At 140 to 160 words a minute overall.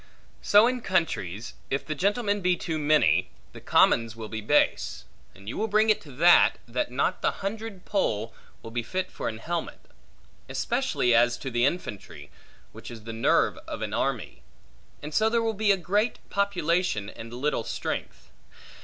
No: average, 170 wpm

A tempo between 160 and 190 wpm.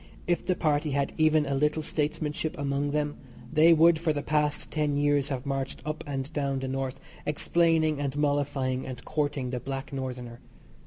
Yes: average, 175 wpm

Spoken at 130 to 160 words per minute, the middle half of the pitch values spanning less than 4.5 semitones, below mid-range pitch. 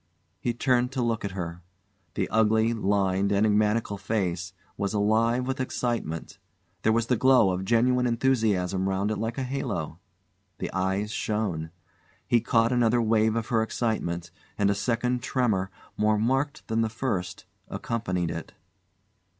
Yes: average, 150 wpm; average, 3.5 semitones; low, 110 Hz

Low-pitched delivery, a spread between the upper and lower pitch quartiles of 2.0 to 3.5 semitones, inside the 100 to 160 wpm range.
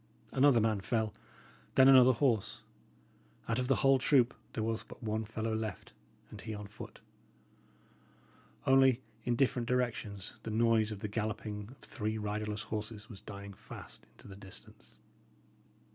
Yes: low, 110 Hz; average, 2.9 semitones; average, 150 wpm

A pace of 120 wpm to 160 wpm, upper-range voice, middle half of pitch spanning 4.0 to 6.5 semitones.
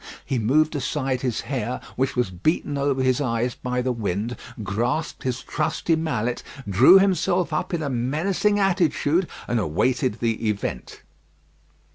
No: average, 145 wpm; low, 130 Hz; average, 4.8 semitones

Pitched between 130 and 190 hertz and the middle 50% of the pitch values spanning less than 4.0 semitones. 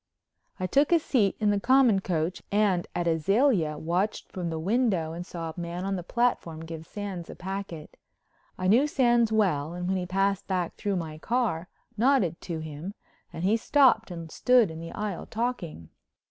No: medium, 185 Hz; average, 4.7 semitones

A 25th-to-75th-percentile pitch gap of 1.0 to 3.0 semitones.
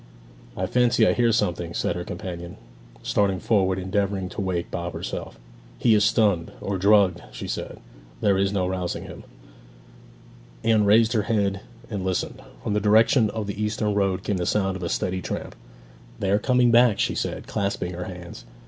Yes: narrow, 2.6 semitones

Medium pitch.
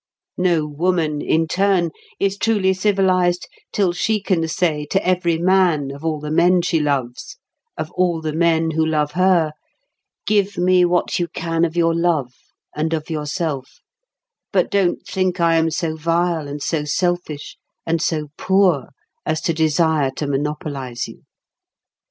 Yes: medium, 165 Hz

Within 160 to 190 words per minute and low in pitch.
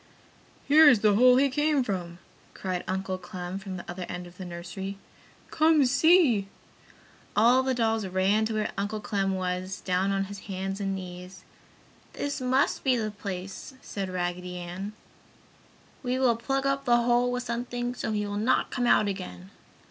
No: average, 170 wpm; high, 205 Hz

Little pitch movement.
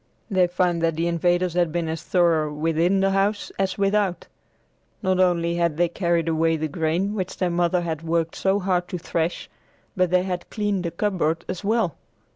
Yes: narrow, 2.1 semitones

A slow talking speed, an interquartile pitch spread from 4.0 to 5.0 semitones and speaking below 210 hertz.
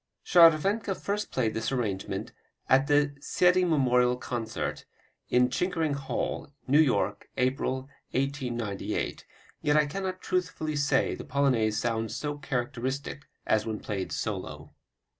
Yes: slow, 120 wpm; average, 4.3 semitones; low, 135 Hz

